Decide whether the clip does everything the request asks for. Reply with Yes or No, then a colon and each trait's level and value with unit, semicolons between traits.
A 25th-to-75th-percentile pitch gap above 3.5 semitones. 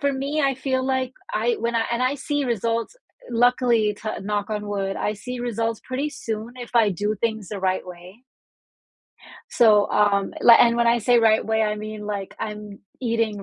No: average, 2.8 semitones